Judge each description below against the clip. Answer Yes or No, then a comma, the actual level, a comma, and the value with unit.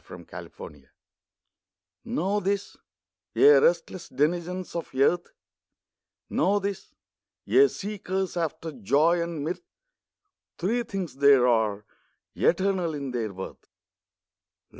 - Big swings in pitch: Yes, wide, 5.7 semitones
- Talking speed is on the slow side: Yes, slow, 100 wpm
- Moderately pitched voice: Yes, medium, 170 Hz